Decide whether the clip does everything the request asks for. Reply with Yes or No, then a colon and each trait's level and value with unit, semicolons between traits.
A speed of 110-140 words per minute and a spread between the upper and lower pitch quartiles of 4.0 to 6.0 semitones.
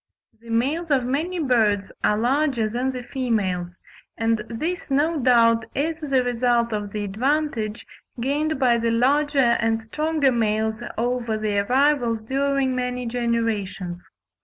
No: slow, 135 wpm; average, 3.6 semitones